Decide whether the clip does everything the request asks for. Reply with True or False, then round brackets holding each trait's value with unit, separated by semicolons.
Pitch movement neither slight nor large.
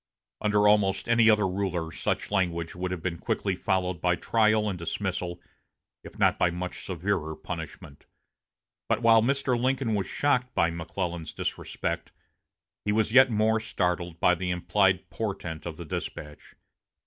True (3.8 semitones)